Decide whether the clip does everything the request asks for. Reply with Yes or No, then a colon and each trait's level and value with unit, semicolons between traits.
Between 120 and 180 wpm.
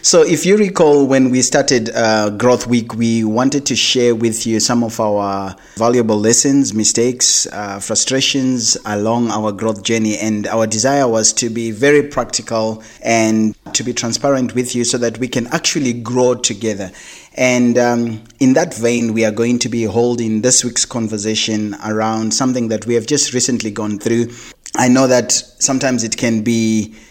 Yes: average, 175 wpm